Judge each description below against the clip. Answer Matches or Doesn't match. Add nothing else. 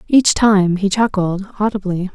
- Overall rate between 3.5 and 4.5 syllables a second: Matches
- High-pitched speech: Matches